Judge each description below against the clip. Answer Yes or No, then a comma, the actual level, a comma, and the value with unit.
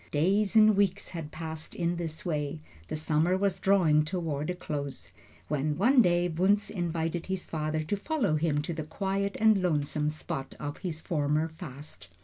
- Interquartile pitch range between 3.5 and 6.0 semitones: Yes, average, 3.8 semitones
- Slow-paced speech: No, average, 170 wpm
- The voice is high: No, medium, 165 Hz